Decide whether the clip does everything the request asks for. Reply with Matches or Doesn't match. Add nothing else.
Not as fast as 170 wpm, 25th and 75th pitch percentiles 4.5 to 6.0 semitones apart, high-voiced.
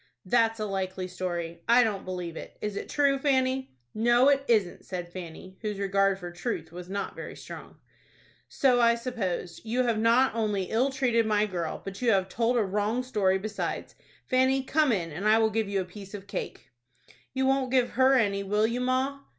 Doesn't match